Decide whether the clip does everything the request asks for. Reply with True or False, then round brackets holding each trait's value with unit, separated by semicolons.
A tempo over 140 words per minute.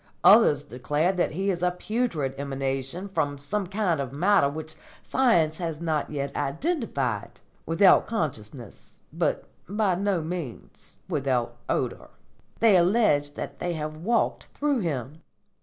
False (135 wpm)